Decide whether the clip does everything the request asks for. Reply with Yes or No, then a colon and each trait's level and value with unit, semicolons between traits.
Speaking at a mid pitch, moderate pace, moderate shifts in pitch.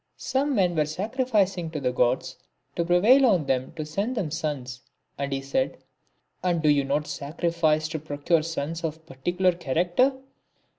Yes: medium, 165 Hz; average, 180 wpm; average, 4.1 semitones